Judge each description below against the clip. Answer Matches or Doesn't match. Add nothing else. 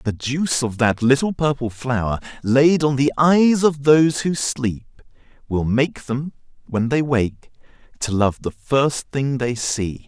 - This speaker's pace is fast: Doesn't match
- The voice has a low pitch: Matches